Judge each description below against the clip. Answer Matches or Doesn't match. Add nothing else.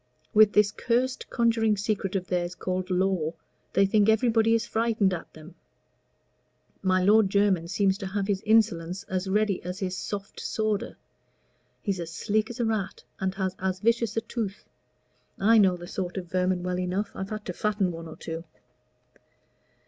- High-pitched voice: Matches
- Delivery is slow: Doesn't match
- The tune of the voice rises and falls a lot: Doesn't match